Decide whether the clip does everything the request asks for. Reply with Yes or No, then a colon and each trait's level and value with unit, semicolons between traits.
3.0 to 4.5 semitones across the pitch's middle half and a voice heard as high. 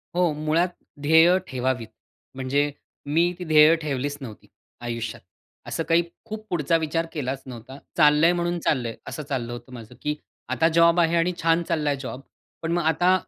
No: average, 4.1 semitones; medium, 155 Hz